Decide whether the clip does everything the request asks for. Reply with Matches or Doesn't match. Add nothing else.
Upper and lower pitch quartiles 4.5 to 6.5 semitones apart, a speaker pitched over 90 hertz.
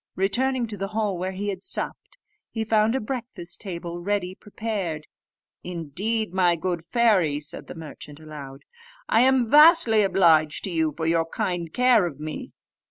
Matches